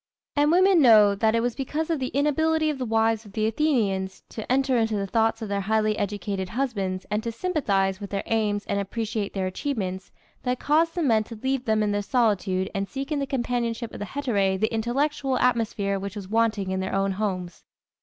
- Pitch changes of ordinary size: Yes, average, 4.7 semitones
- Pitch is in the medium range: No, high, 220 Hz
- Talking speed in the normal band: No, fast, 215 wpm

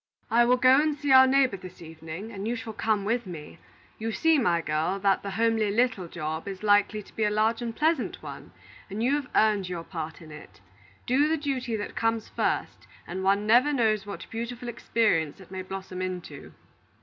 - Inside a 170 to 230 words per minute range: Yes, fast, 205 wpm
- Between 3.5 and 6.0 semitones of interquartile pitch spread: Yes, average, 4.5 semitones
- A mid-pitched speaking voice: No, high, 215 Hz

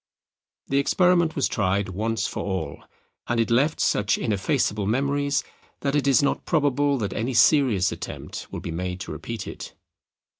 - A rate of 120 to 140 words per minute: No, average, 160 wpm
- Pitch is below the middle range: Yes, low, 120 Hz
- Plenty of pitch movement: Yes, wide, 5.8 semitones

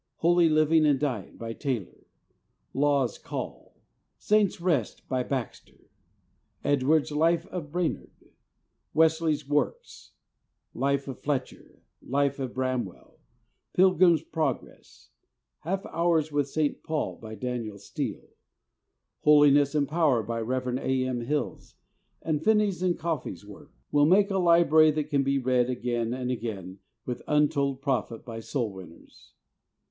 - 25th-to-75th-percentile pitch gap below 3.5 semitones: No, average, 4.1 semitones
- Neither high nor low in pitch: Yes, medium, 145 Hz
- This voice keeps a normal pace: No, slow, 130 wpm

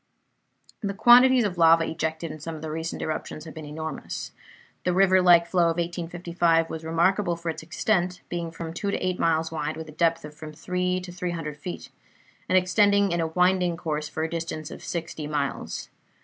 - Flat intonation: Yes, narrow, 2.2 semitones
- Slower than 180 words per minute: No, average, 200 wpm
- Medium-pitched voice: Yes, medium, 170 Hz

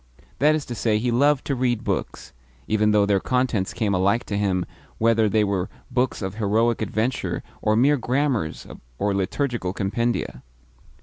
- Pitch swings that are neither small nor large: Yes, average, 3.6 semitones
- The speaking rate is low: No, average, 165 wpm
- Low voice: Yes, low, 110 Hz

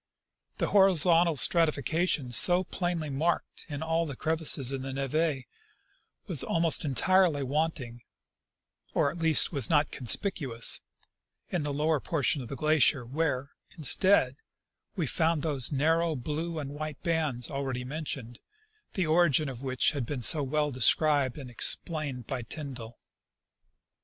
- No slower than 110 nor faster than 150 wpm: Yes, slow, 135 wpm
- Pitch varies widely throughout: No, average, 3.5 semitones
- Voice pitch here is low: No, medium, 150 Hz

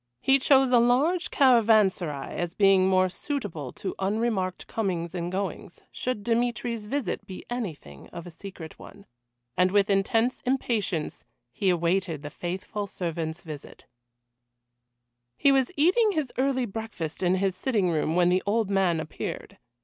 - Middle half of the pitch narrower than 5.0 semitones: No, average, 5.3 semitones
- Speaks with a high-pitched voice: Yes, high, 195 Hz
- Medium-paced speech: Yes, average, 145 wpm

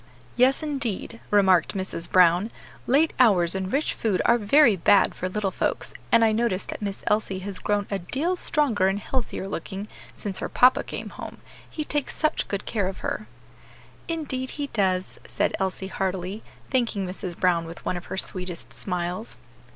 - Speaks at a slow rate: No, average, 175 wpm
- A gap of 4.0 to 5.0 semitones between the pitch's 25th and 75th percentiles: Yes, average, 4.6 semitones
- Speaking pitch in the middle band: No, high, 200 Hz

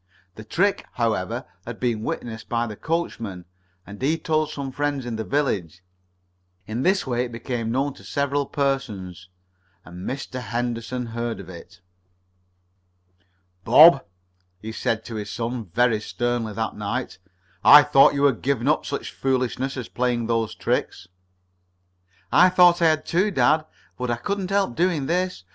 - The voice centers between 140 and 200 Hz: No, low, 125 Hz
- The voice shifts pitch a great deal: No, average, 4.4 semitones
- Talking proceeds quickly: No, average, 155 wpm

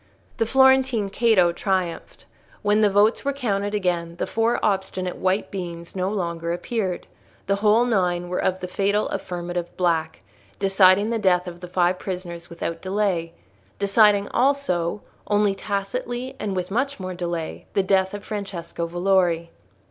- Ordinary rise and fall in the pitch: Yes, average, 3.0 semitones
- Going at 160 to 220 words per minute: No, average, 150 wpm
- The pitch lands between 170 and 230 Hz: Yes, high, 190 Hz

